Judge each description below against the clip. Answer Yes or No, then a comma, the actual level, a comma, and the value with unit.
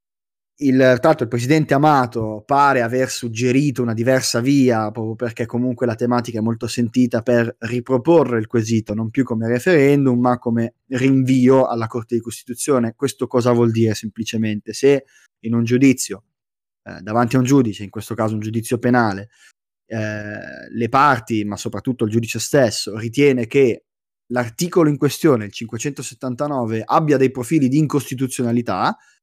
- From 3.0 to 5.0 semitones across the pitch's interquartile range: No, narrow, 2.5 semitones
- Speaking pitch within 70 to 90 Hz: No, low, 120 Hz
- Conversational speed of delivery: Yes, average, 150 wpm